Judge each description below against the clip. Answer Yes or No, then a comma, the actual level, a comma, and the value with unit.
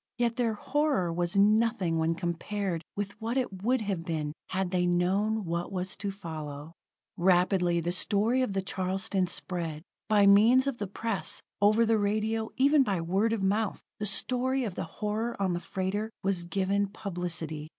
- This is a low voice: No, high, 195 Hz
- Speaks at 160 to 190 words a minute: Yes, average, 170 wpm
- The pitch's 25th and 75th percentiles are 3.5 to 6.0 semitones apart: Yes, average, 3.9 semitones